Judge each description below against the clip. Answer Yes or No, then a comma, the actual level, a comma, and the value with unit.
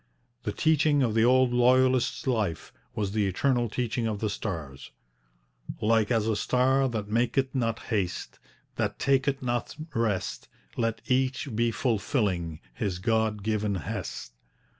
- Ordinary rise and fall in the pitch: Yes, average, 3.7 semitones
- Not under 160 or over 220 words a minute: No, average, 140 wpm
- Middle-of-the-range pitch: No, low, 115 Hz